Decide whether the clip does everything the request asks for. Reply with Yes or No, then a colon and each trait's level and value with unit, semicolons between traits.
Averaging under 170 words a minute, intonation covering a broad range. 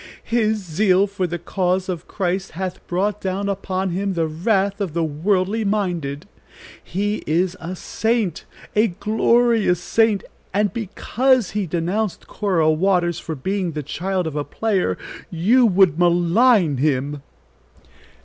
No: average, 140 wpm; average, 3.5 semitones